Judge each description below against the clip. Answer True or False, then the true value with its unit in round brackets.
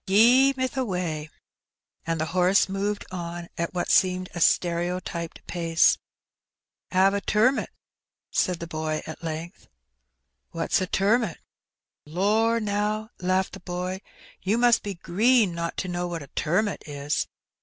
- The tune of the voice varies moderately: True (3.6 semitones)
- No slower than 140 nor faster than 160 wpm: True (155 wpm)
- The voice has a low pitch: False (185 Hz)